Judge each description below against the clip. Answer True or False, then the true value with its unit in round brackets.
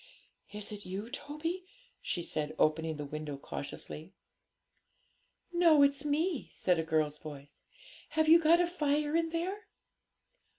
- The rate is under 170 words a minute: True (135 wpm)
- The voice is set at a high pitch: True (280 Hz)